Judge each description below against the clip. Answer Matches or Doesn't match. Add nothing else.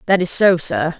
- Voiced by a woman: Matches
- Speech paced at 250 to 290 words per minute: Doesn't match